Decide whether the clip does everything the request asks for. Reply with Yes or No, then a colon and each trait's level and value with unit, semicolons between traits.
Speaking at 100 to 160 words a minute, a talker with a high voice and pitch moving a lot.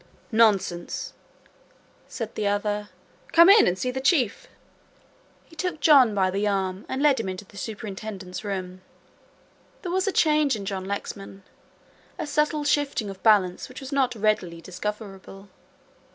Yes: average, 150 wpm; high, 210 Hz; wide, 6.1 semitones